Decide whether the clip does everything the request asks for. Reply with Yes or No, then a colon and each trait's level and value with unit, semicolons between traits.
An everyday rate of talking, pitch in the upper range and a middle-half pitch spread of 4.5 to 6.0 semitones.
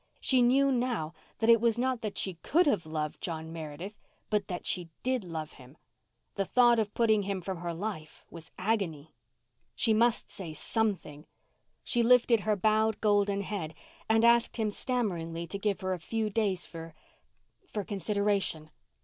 Yes: average, 165 wpm; high, 200 Hz; average, 5.2 semitones